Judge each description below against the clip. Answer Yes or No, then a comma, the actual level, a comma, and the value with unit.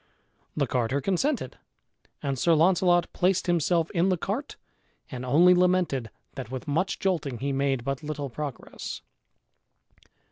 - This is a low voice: No, medium, 155 Hz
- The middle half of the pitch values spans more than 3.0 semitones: Yes, average, 5.0 semitones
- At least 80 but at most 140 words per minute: Yes, slow, 135 wpm